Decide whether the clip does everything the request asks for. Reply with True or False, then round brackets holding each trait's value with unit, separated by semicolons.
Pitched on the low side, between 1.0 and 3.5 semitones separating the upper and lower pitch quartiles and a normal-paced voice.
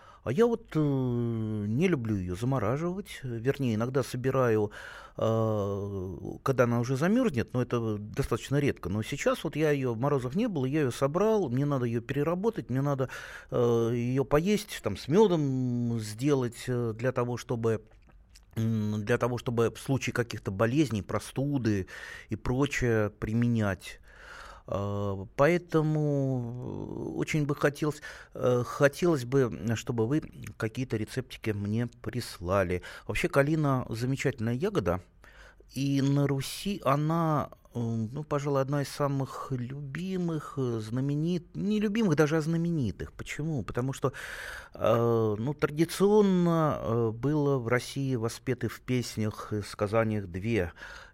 False (125 Hz; 4.4 semitones; 125 wpm)